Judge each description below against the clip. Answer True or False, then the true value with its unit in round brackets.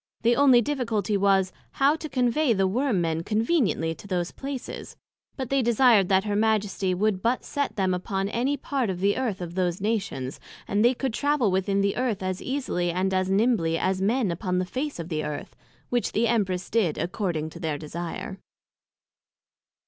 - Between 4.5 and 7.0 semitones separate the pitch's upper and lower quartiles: True (4.8 semitones)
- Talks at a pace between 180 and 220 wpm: True (185 wpm)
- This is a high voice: True (200 Hz)